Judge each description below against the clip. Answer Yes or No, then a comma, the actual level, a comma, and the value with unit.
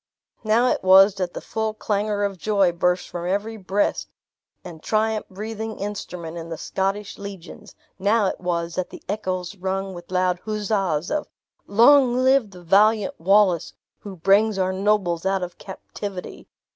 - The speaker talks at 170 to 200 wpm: No, average, 160 wpm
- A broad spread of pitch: No, average, 2.8 semitones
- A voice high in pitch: Yes, high, 195 Hz